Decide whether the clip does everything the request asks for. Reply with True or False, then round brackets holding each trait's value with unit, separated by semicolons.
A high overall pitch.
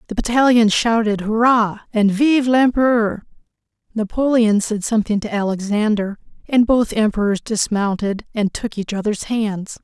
True (220 Hz)